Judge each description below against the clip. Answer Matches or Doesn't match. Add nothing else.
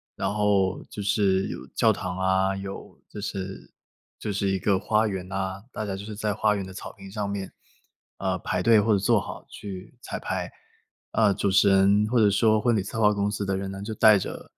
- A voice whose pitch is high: Doesn't match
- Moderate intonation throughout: Doesn't match